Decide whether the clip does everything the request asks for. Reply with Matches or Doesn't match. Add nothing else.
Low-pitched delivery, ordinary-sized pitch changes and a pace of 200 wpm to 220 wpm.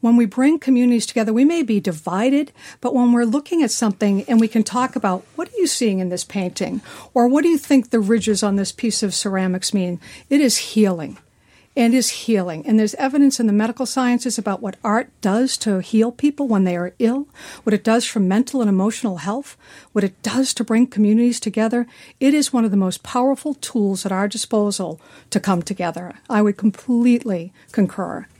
Doesn't match